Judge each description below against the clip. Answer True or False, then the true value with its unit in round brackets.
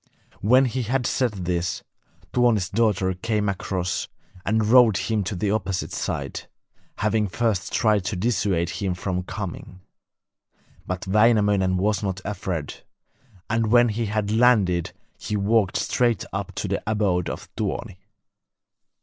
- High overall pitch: False (105 Hz)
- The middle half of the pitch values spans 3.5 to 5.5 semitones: False (3.1 semitones)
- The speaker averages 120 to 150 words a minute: True (135 wpm)